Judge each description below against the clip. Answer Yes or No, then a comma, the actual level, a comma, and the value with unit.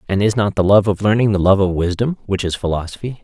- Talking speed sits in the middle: No, fast, 260 wpm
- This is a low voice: Yes, low, 100 Hz